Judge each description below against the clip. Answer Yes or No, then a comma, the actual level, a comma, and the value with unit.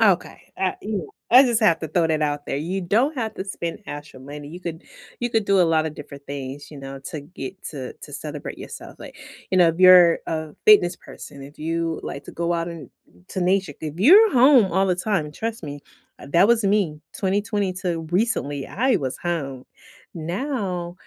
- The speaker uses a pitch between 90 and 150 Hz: No, medium, 175 Hz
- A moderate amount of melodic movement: Yes, average, 4.8 semitones